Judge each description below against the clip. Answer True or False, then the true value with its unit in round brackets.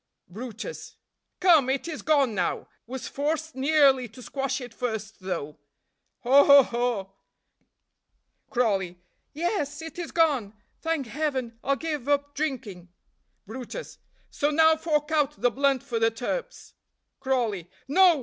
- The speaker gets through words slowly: True (130 wpm)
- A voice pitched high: True (270 Hz)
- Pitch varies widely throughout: False (4.8 semitones)